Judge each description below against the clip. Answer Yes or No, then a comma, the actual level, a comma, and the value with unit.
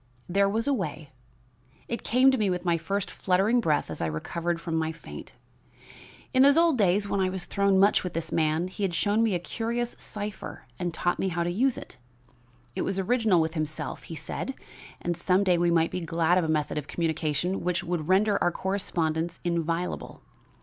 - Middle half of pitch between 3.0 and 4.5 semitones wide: Yes, average, 3.6 semitones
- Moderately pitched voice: Yes, medium, 180 Hz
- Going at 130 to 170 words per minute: No, fast, 205 wpm